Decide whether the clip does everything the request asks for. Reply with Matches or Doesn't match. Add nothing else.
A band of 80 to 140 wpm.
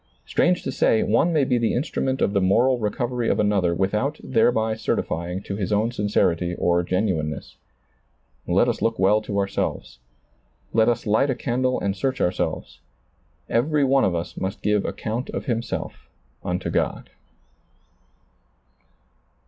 Doesn't match